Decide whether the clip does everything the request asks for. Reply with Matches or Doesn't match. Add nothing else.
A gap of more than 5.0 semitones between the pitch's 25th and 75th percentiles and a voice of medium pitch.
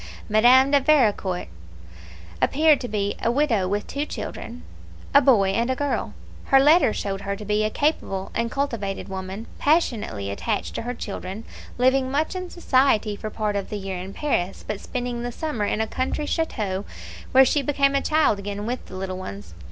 Doesn't match